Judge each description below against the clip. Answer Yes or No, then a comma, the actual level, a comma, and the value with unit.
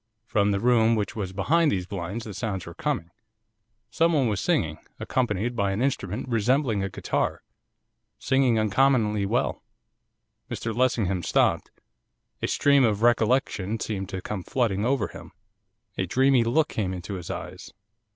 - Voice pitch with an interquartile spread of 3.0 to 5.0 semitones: Yes, average, 4.5 semitones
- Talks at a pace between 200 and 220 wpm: No, average, 150 wpm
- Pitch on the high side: No, low, 110 Hz